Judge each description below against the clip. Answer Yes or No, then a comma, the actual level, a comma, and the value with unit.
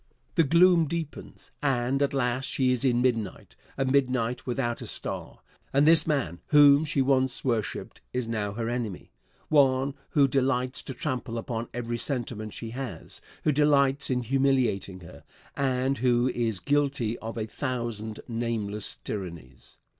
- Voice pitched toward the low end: Yes, low, 125 Hz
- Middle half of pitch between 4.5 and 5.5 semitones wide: No, average, 3.2 semitones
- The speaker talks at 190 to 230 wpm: No, average, 150 wpm